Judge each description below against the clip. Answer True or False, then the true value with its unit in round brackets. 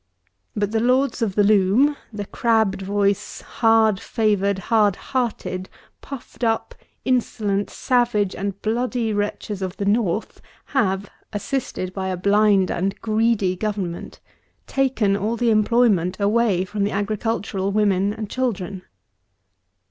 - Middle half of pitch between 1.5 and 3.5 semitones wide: True (2.6 semitones)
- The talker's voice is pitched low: False (210 Hz)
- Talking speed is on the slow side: True (125 wpm)